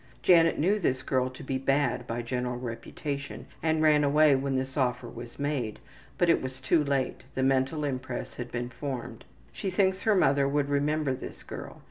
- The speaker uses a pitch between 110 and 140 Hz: Yes, low, 135 Hz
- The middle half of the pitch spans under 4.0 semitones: Yes, average, 2.9 semitones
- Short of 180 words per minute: No, average, 185 wpm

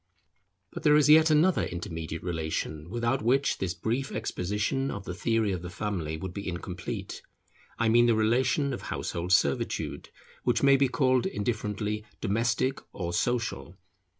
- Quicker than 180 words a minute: No, average, 150 wpm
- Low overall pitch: Yes, low, 110 Hz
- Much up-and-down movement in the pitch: Yes, wide, 6.2 semitones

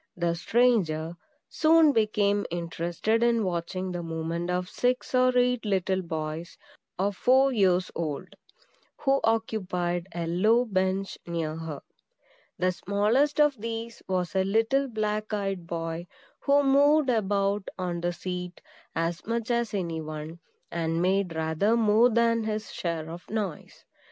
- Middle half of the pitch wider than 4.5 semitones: Yes, average, 5.0 semitones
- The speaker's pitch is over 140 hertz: Yes, high, 190 Hz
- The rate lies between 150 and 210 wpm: No, average, 140 wpm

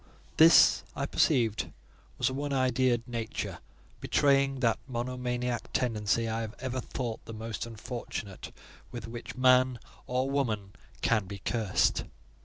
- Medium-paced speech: No, slow, 130 wpm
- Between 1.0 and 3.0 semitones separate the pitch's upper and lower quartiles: Yes, narrow, 2.4 semitones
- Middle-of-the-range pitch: No, low, 120 Hz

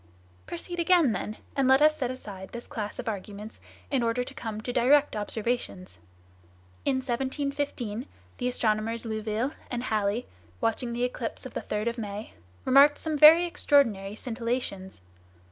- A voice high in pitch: Yes, high, 235 Hz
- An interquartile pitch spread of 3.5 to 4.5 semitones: Yes, average, 3.8 semitones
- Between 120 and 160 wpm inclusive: Yes, average, 150 wpm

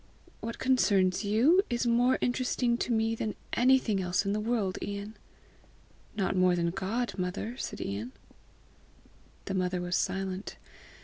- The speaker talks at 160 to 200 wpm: No, average, 145 wpm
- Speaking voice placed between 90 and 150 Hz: No, high, 210 Hz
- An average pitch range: Yes, average, 4.4 semitones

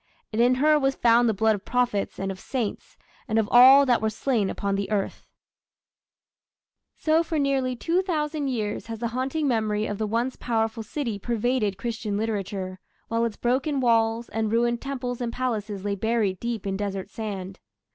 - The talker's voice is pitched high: Yes, high, 230 Hz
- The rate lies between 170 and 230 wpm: Yes, average, 180 wpm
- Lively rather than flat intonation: No, average, 3.5 semitones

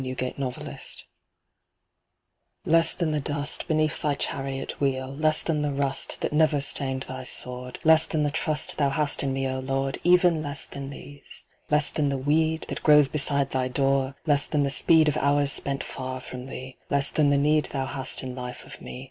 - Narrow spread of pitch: Yes, narrow, 2.2 semitones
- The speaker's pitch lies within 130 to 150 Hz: Yes, medium, 140 Hz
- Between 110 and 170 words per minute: No, average, 200 wpm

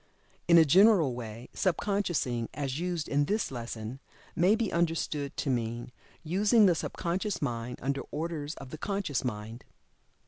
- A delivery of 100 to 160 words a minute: Yes, average, 150 wpm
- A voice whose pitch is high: No, medium, 150 Hz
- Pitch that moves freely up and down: Yes, wide, 6.4 semitones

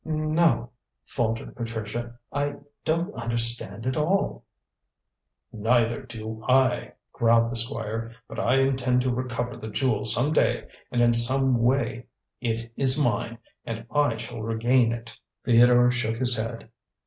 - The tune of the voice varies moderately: No, narrow, 2.1 semitones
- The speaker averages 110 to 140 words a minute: Yes, slow, 135 wpm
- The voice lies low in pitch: Yes, low, 120 Hz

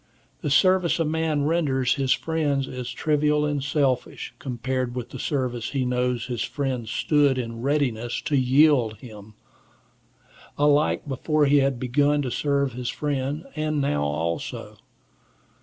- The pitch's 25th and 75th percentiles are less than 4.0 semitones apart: Yes, average, 3.0 semitones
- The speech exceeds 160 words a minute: No, average, 140 wpm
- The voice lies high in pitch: No, low, 135 Hz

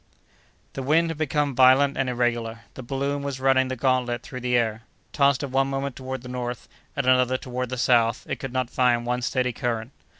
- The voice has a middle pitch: No, low, 130 Hz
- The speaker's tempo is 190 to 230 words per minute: Yes, fast, 205 wpm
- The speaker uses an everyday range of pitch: No, narrow, 1.8 semitones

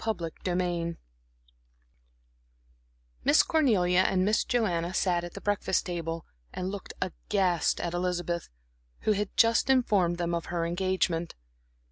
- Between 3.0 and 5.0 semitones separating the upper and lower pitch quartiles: No, narrow, 2.6 semitones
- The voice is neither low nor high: Yes, medium, 180 Hz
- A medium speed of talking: No, slow, 125 wpm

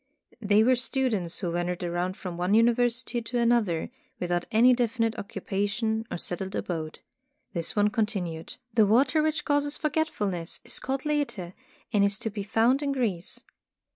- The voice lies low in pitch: No, high, 220 Hz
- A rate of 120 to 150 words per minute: No, average, 160 wpm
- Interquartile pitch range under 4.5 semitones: No, average, 5.3 semitones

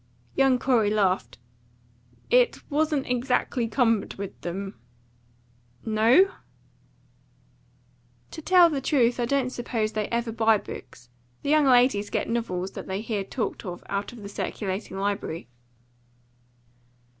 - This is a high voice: Yes, high, 230 Hz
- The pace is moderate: No, slow, 125 wpm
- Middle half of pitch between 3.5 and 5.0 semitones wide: Yes, average, 4.4 semitones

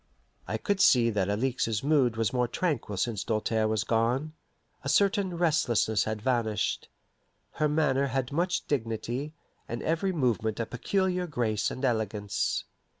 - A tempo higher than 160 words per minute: No, average, 145 wpm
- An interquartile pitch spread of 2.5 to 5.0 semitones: No, wide, 5.6 semitones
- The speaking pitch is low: Yes, low, 125 Hz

